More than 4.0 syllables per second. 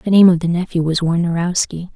Yes: 6.0 syllables/s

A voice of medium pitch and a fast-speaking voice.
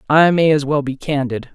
Yes: medium, 145 Hz; fast, 235 wpm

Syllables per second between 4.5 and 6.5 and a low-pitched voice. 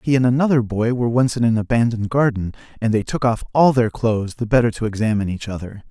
No: 6.7 syllables/s; low, 115 Hz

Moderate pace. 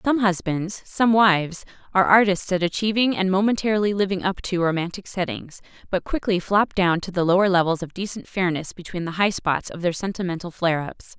Yes: average, 190 wpm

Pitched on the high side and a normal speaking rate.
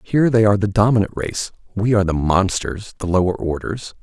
No: low, 100 Hz; average, 165 wpm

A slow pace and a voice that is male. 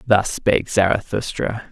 Yes: slow, 105 wpm; male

